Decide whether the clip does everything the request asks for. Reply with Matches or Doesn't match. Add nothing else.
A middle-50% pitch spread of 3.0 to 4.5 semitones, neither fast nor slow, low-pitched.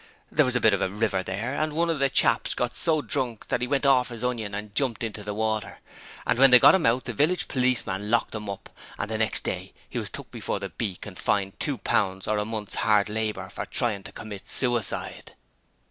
Doesn't match